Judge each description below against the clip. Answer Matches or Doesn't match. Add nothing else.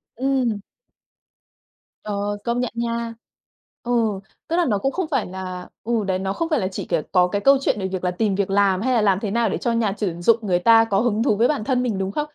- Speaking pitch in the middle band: Doesn't match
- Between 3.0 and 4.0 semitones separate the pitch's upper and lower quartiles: Matches